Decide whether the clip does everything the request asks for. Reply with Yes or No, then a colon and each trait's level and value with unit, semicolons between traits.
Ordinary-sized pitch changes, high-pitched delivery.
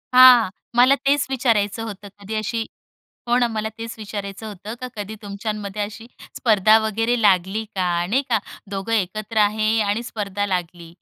No: narrow, 2.2 semitones; high, 215 Hz